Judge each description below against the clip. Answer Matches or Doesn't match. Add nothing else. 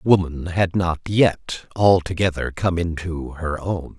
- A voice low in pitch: Matches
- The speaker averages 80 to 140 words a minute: Matches